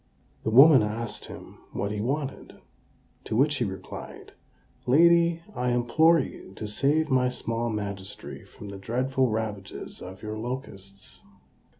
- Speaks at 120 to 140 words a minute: Yes, slow, 135 wpm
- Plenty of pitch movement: No, average, 4.3 semitones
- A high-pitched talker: No, low, 120 Hz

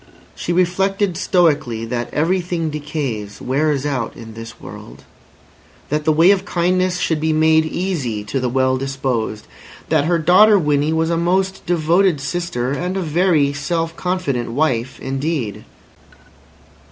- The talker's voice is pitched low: No, medium, 155 Hz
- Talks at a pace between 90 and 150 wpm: Yes, average, 140 wpm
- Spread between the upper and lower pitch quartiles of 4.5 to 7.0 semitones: Yes, average, 5.0 semitones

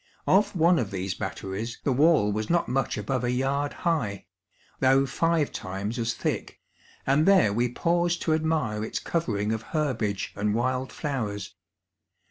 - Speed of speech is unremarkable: Yes, average, 155 wpm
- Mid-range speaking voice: No, low, 125 Hz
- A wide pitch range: Yes, wide, 6.9 semitones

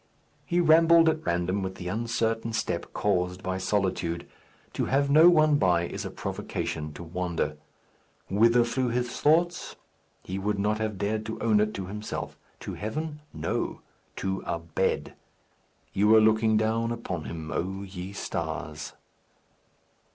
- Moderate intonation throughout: Yes, average, 4.4 semitones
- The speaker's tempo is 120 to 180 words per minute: Yes, average, 150 wpm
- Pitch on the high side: No, low, 105 Hz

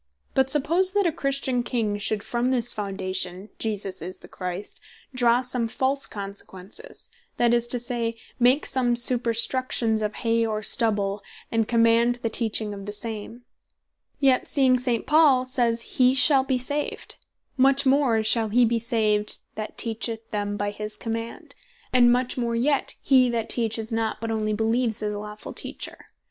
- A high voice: Yes, high, 230 Hz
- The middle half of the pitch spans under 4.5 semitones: Yes, average, 3.0 semitones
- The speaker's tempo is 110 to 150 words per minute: No, average, 160 wpm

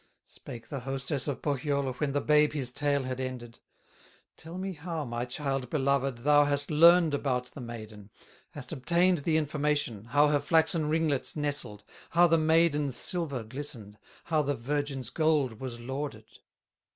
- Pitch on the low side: No, medium, 145 Hz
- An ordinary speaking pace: Yes, average, 155 wpm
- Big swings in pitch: No, average, 3.3 semitones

